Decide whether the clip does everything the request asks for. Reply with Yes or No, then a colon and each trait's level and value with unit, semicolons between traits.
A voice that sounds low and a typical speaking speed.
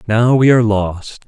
Yes: low, 110 Hz; average, 190 wpm